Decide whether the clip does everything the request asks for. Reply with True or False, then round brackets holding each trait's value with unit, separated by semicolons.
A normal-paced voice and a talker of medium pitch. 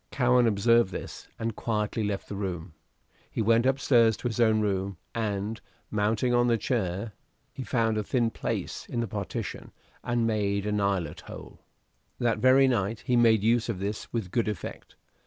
False (175 wpm; 110 Hz)